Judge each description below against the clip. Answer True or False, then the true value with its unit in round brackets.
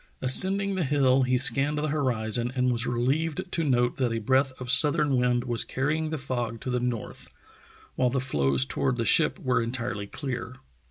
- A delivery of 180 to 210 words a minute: True (185 wpm)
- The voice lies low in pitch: True (130 Hz)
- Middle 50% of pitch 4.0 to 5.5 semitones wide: False (2.9 semitones)